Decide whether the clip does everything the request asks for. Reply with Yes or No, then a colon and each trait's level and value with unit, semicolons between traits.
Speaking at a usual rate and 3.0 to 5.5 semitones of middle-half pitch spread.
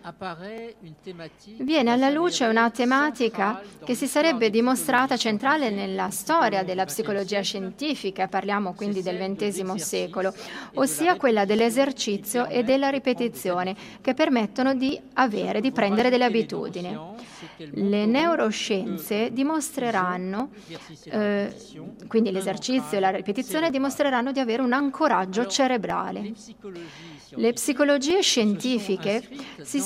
No: slow, 105 wpm; average, 5.0 semitones